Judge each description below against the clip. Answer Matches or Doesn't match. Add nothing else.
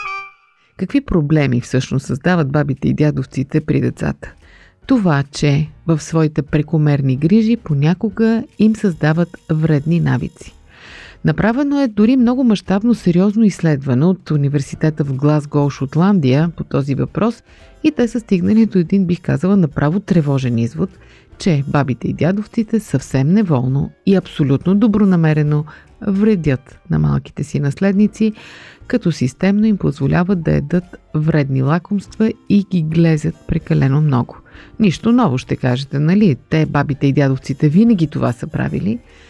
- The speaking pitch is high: Doesn't match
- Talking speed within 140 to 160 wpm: Doesn't match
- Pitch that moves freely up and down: Matches